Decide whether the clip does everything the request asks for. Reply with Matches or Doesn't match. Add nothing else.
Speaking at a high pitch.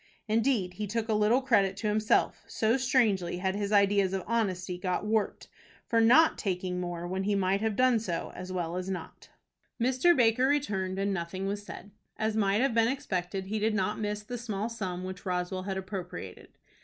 Matches